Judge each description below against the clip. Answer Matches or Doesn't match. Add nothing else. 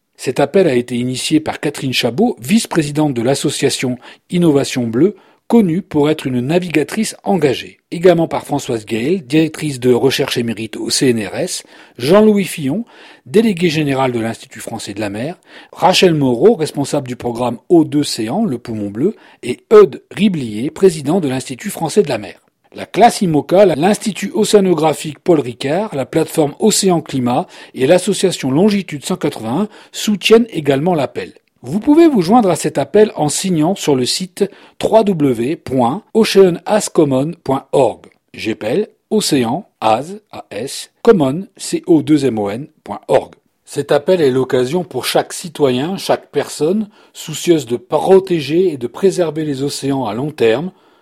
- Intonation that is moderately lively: Doesn't match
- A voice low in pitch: Doesn't match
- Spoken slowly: Matches